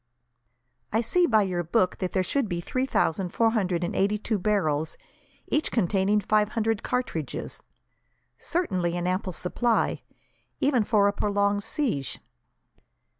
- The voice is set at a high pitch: Yes, high, 205 Hz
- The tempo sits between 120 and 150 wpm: Yes, average, 140 wpm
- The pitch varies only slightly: No, average, 3.9 semitones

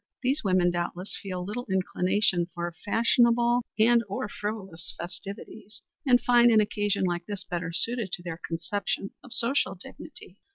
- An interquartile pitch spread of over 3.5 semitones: Yes, average, 4.7 semitones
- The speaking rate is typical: Yes, average, 150 wpm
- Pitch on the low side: No, high, 200 Hz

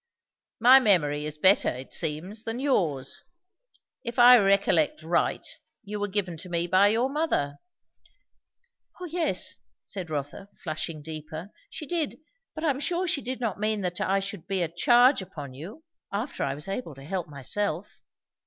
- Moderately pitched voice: No, high, 195 Hz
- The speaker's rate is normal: Yes, average, 165 wpm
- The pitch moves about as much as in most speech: No, wide, 7.3 semitones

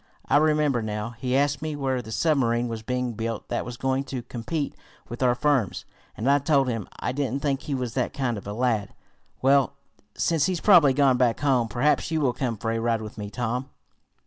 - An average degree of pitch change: Yes, average, 3.4 semitones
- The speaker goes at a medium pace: No, fast, 215 wpm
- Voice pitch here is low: Yes, low, 125 Hz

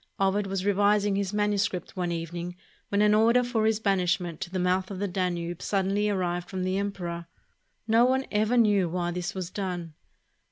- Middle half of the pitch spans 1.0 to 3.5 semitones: Yes, narrow, 2.6 semitones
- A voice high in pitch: Yes, high, 195 Hz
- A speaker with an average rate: Yes, average, 190 wpm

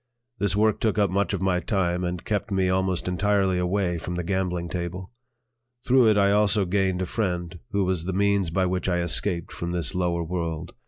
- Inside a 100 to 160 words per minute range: No, fast, 205 wpm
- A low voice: Yes, very low, 95 Hz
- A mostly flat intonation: Yes, narrow, 2.2 semitones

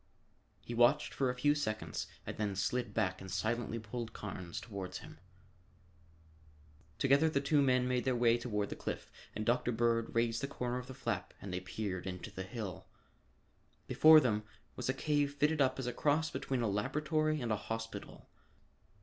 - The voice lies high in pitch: No, low, 120 Hz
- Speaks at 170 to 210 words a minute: Yes, average, 180 wpm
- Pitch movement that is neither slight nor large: Yes, average, 4.3 semitones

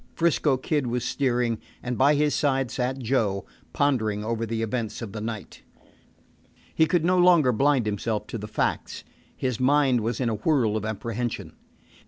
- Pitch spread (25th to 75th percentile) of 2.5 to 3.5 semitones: No, average, 4.2 semitones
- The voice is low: Yes, low, 125 Hz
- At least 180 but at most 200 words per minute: No, average, 170 wpm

